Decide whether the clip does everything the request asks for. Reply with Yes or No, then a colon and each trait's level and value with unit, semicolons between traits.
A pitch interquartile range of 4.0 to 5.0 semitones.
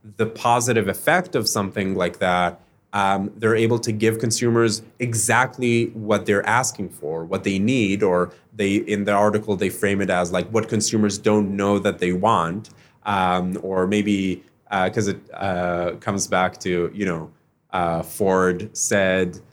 No: average, 3.3 semitones